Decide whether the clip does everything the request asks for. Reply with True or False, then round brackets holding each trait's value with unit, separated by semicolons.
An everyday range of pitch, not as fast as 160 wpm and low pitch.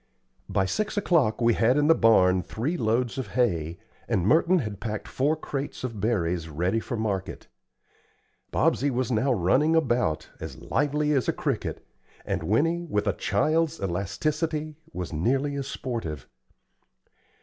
False (7.1 semitones; 150 wpm; 120 Hz)